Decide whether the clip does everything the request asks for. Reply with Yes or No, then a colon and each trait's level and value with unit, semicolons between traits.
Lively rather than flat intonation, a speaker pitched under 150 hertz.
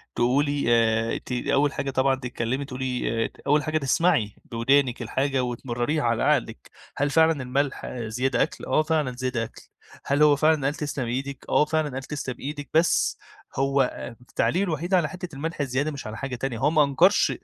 No: average, 3.1 semitones; low, 135 Hz